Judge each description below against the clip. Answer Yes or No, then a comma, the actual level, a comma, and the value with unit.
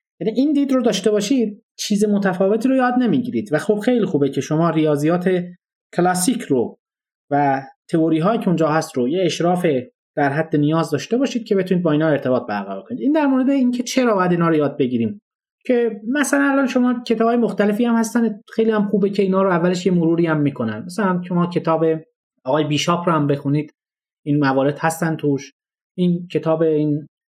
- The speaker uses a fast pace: Yes, fast, 185 wpm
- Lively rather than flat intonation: Yes, wide, 6.7 semitones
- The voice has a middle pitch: Yes, medium, 180 Hz